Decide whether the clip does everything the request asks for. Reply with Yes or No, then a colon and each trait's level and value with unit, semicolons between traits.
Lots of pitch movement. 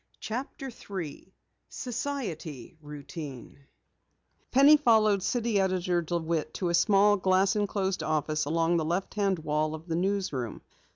No: average, 4.7 semitones